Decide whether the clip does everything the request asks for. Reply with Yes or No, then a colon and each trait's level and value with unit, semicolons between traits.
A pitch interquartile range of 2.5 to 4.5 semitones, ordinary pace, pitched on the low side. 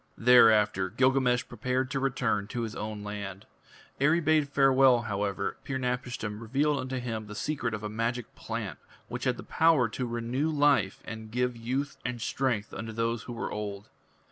Yes: average, 3.6 semitones; average, 170 wpm; low, 120 Hz